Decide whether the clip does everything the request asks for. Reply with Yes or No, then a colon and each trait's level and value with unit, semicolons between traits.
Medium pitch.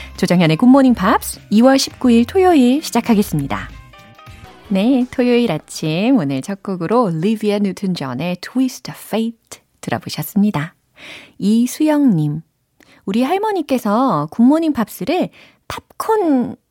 No: high, 225 Hz